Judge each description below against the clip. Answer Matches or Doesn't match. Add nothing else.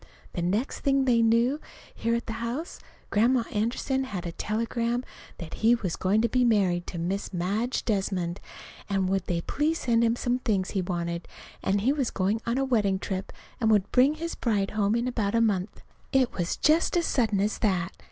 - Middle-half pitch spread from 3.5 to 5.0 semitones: Matches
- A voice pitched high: Matches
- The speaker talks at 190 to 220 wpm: Matches